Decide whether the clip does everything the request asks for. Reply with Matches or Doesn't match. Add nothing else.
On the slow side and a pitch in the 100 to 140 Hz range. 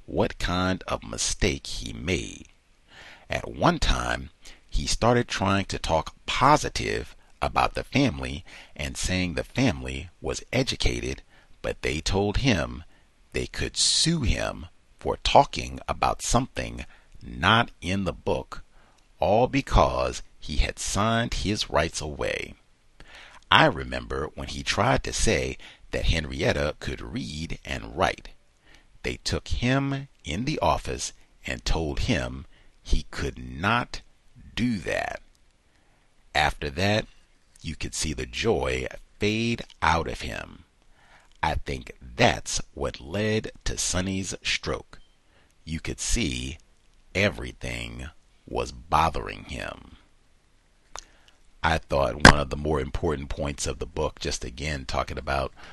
Doesn't match